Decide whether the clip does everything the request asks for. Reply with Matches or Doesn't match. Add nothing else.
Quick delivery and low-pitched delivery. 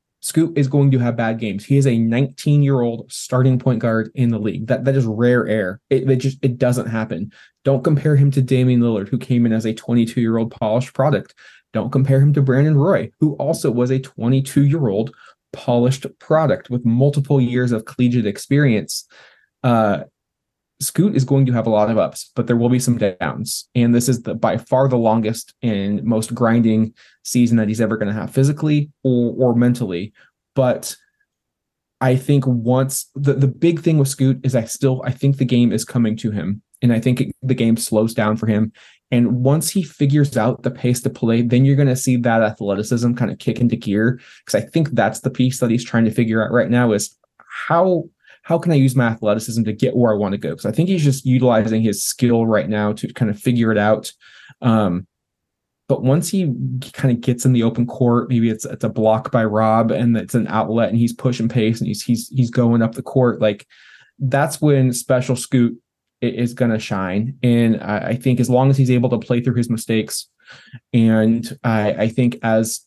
Matches